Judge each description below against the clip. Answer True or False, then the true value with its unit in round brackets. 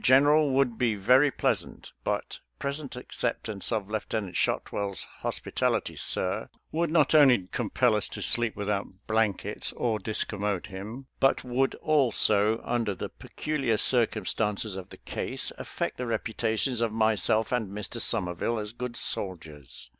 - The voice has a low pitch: True (110 Hz)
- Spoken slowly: False (145 wpm)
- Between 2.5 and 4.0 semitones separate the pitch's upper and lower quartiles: True (3.5 semitones)